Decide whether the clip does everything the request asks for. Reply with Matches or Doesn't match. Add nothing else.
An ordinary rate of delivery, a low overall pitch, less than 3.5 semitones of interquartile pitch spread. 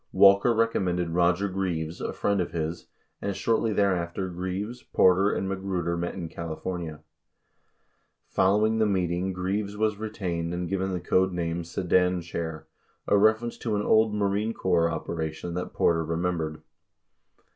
Matches